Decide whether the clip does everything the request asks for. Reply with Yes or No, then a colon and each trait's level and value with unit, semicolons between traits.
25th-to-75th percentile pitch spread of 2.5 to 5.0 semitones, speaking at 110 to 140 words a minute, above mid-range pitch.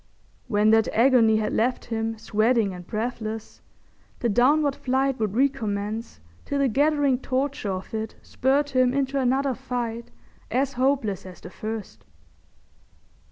Yes: average, 3.6 semitones; slow, 135 wpm; high, 240 Hz